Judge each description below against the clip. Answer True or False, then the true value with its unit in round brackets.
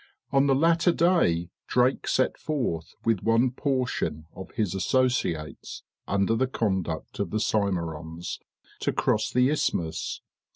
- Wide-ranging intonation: True (7.3 semitones)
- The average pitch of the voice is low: True (110 Hz)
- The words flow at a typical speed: False (130 wpm)